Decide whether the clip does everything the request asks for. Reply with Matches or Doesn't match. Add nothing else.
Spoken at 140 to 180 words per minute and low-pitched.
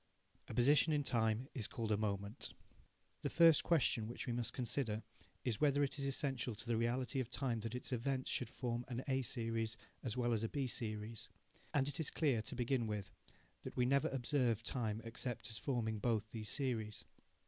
Doesn't match